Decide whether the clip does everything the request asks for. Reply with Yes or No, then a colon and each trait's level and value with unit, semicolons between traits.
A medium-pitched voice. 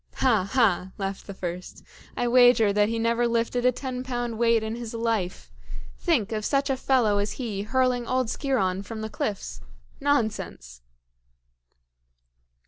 No: high, 230 Hz